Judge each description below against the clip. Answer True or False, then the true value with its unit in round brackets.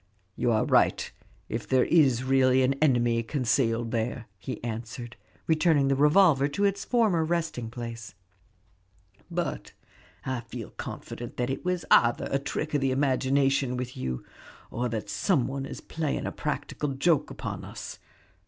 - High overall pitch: False (130 Hz)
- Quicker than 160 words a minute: False (155 wpm)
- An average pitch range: True (3.8 semitones)